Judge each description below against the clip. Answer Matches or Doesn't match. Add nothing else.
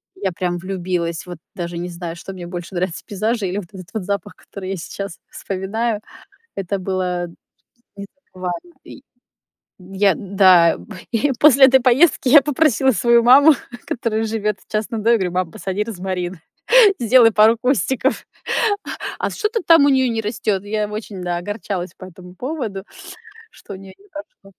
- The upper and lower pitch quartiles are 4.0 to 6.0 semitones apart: Matches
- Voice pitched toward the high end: Matches